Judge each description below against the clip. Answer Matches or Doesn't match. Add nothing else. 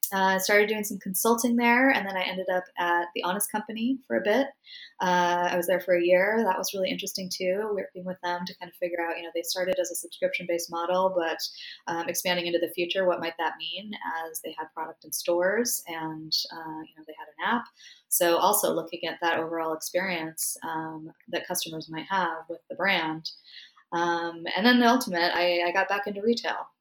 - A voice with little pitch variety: Matches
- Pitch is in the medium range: Matches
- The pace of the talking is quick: Matches